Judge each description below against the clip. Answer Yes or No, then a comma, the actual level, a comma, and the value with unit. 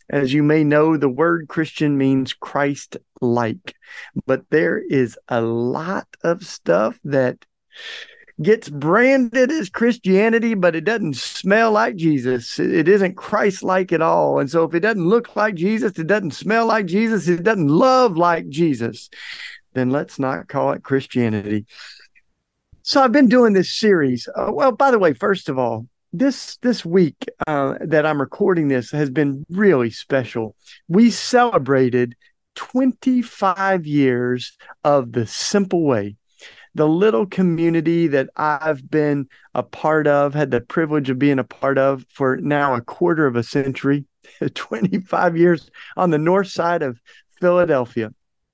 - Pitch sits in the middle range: Yes, medium, 160 Hz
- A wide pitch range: Yes, wide, 7.2 semitones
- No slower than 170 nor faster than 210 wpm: No, average, 155 wpm